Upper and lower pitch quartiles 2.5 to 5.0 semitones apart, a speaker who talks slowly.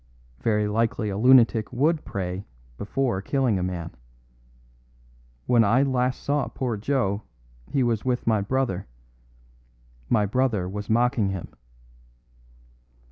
Yes: average, 4.2 semitones; slow, 120 wpm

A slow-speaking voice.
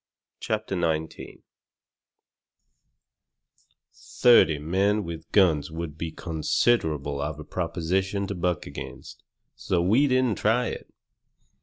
Yes: slow, 105 wpm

